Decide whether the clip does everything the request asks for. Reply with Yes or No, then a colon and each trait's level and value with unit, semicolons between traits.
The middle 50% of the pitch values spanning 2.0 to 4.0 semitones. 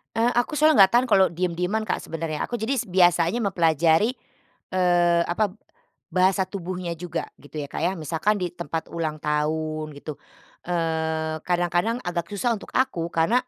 Yes: average, 3.3 semitones